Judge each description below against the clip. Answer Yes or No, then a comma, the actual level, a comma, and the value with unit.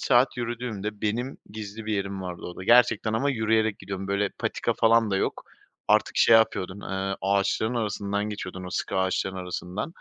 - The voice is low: Yes, low, 105 Hz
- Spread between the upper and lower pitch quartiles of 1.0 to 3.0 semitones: Yes, narrow, 2.6 semitones